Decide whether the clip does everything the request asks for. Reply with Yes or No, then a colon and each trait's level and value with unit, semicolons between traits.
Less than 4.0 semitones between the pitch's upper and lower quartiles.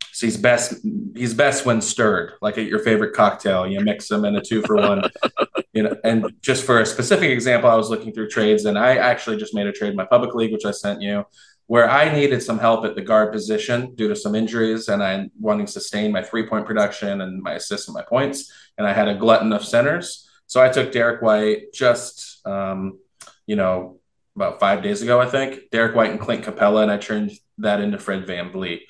Yes: average, 2.8 semitones